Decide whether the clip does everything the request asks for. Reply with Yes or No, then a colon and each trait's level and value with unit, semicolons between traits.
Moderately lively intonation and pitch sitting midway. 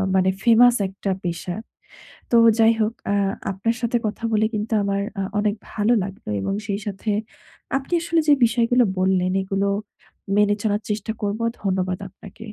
No: average, 3.0 semitones; high, 210 Hz